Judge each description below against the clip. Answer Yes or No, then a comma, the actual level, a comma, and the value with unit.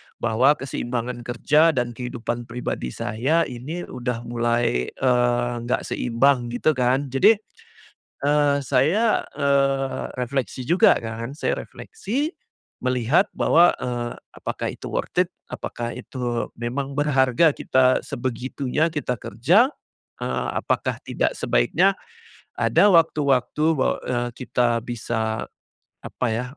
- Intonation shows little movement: No, average, 3.4 semitones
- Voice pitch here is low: Yes, low, 125 Hz